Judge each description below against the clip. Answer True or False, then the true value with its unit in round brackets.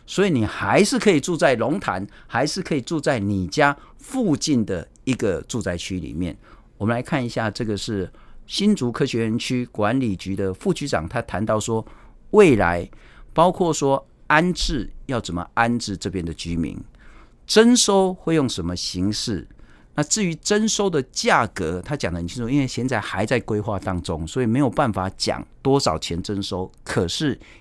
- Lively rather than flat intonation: True (6.9 semitones)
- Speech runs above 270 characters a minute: False (255 characters per minute)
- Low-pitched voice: True (115 Hz)